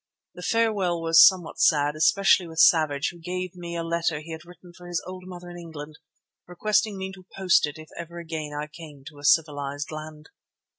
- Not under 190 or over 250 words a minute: Yes, average, 200 wpm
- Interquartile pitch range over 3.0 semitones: No, average, 2.7 semitones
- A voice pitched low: No, medium, 170 Hz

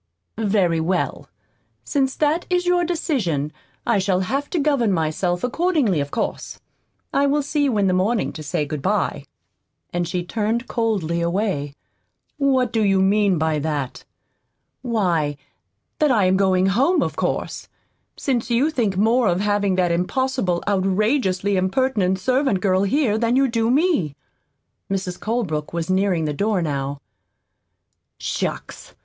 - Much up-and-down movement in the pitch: Yes, wide, 6.2 semitones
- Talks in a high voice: Yes, high, 200 Hz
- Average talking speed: Yes, average, 145 wpm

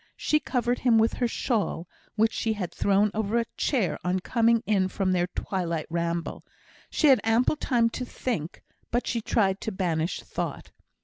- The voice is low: No, high, 215 Hz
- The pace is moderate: Yes, average, 175 wpm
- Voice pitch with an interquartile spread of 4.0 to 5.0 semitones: Yes, average, 4.4 semitones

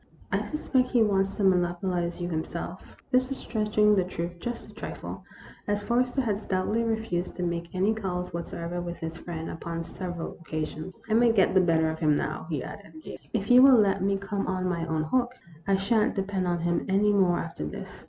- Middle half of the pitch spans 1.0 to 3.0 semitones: No, average, 3.6 semitones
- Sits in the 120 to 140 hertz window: No, medium, 185 Hz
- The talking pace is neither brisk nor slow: No, fast, 210 wpm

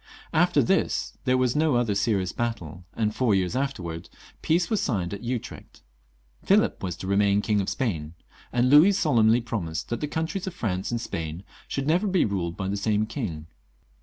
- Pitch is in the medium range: No, low, 110 Hz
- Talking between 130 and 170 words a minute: No, average, 185 wpm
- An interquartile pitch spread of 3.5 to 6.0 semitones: Yes, wide, 5.6 semitones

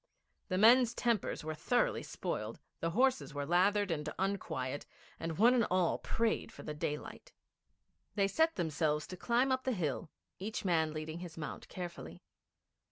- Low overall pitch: No, medium, 185 Hz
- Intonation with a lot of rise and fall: Yes, wide, 6.6 semitones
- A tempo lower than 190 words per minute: Yes, average, 160 wpm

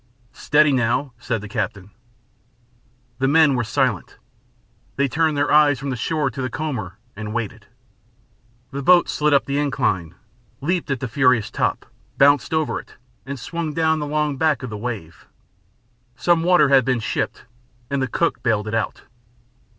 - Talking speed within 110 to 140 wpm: No, average, 165 wpm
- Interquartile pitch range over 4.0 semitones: Yes, average, 4.4 semitones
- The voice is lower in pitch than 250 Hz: Yes, low, 135 Hz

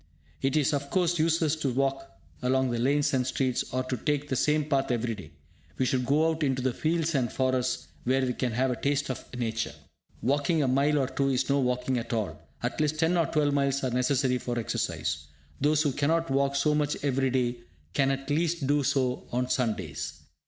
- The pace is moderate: No, fast, 210 wpm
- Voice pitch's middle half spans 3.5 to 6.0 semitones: No, average, 2.7 semitones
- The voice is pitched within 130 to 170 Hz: Yes, low, 135 Hz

